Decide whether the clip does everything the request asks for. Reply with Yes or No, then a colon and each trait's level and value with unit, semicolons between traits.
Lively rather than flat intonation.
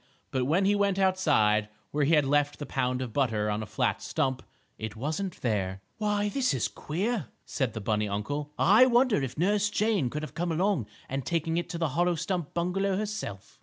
Yes: wide, 7.5 semitones